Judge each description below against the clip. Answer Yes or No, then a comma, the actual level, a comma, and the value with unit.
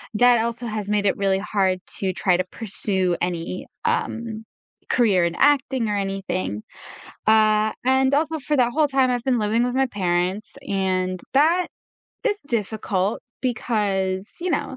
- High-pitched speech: Yes, high, 215 Hz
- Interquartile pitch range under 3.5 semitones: No, average, 4.7 semitones